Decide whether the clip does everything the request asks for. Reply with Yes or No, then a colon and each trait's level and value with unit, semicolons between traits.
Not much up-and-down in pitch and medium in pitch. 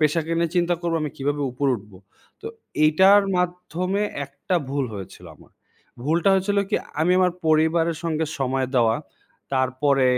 No: average, 4.5 semitones; medium, 155 Hz